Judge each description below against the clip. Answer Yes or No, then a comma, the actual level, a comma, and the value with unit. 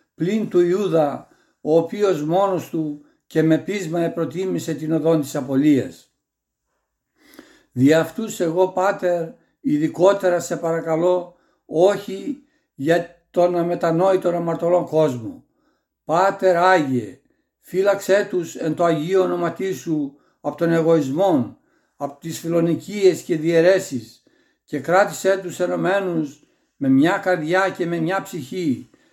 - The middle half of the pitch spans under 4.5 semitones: Yes, average, 2.9 semitones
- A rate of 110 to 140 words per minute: Yes, slow, 115 wpm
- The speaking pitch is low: No, medium, 175 Hz